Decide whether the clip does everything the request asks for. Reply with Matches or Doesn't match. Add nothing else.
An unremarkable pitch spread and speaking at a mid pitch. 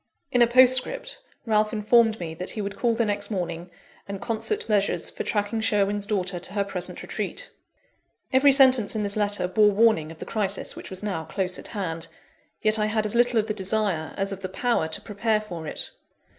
Doesn't match